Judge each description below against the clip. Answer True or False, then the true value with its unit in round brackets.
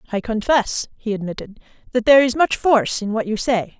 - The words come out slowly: False (205 wpm)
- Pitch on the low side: False (230 Hz)